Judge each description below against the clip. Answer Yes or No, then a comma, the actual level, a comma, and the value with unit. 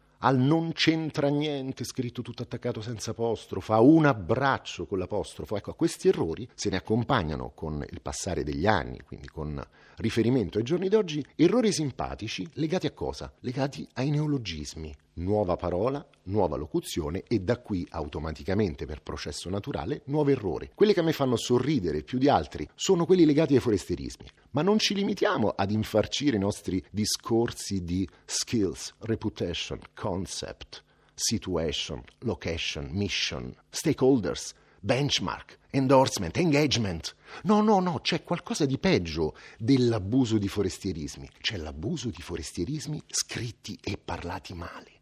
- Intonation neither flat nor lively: No, wide, 7.6 semitones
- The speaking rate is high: No, average, 140 wpm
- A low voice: Yes, low, 115 Hz